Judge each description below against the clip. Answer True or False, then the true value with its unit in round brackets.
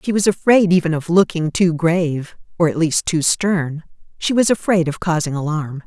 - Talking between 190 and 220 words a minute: True (195 wpm)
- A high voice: False (170 Hz)